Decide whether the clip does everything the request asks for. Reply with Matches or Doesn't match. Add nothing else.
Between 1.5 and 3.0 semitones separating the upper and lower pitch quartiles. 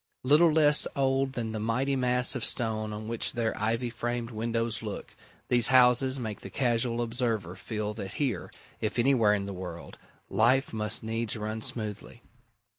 Matches